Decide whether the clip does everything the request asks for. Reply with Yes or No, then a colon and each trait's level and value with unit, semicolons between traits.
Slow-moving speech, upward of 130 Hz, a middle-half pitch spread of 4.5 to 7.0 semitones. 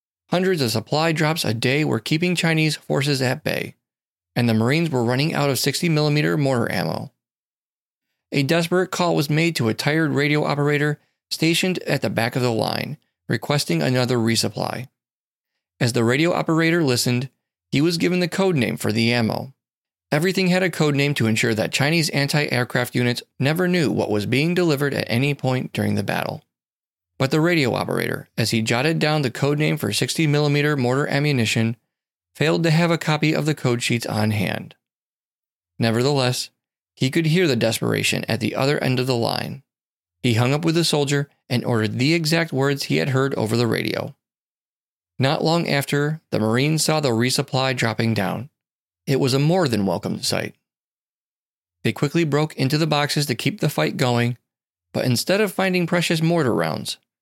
No: average, 180 wpm; medium, 140 Hz; average, 4.9 semitones